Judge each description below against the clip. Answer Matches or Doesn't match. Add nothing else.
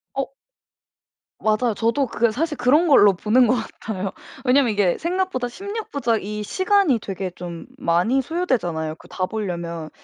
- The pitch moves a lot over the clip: Matches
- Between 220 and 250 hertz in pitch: Matches